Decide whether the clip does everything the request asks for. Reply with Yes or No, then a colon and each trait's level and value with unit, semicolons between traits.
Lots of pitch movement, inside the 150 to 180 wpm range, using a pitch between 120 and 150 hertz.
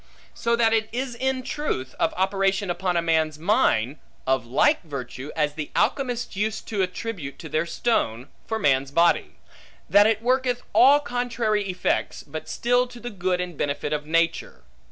No: wide, 7.4 semitones; average, 170 wpm; high, 190 Hz